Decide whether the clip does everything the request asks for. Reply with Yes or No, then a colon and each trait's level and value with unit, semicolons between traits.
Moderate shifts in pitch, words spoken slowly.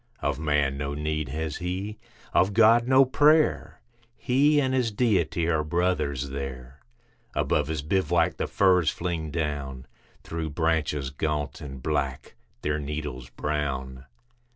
Yes: average, 4.5 semitones; slow, 130 wpm